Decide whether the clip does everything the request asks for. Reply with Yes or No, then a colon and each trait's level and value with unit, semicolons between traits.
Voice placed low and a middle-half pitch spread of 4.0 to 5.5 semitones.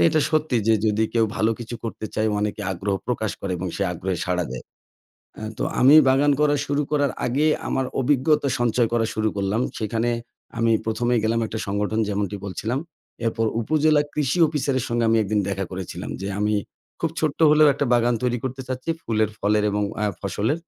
Yes: low, 115 Hz; average, 4.5 semitones